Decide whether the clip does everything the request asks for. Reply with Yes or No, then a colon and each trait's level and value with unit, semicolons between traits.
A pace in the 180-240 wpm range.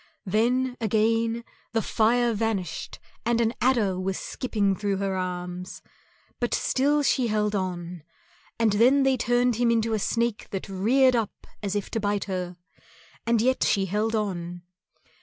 No: average, 155 wpm